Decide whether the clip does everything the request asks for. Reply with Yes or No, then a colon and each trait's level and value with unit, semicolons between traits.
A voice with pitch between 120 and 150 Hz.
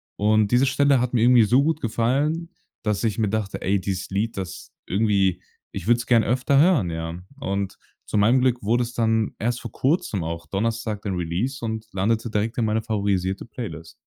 No: low, 110 Hz